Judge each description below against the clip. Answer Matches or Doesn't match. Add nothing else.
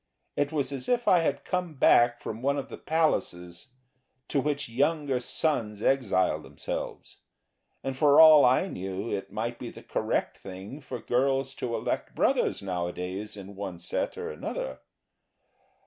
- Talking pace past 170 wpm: Doesn't match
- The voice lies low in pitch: Matches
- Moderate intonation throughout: Doesn't match